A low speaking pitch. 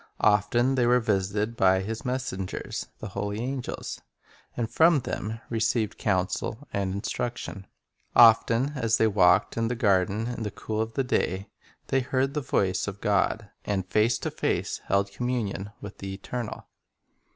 Yes: low, 110 Hz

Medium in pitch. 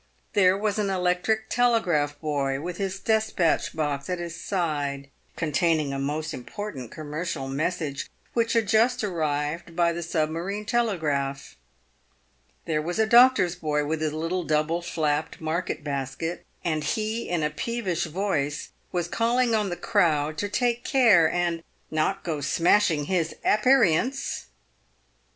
Yes: medium, 170 Hz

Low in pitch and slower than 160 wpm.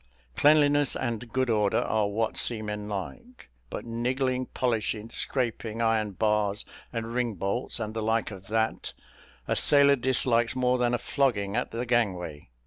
Yes: low, 115 Hz; average, 150 wpm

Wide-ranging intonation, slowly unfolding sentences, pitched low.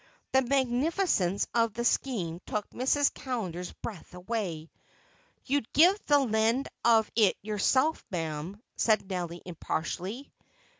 No: wide, 6.3 semitones; slow, 115 wpm; high, 220 Hz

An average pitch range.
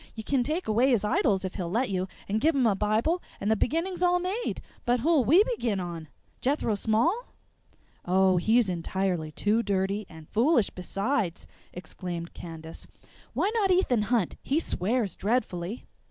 No: wide, 6.8 semitones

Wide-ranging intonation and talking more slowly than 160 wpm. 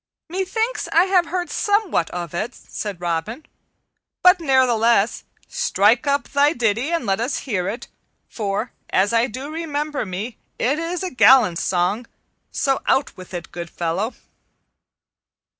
Yes: wide, 7.6 semitones; average, 140 wpm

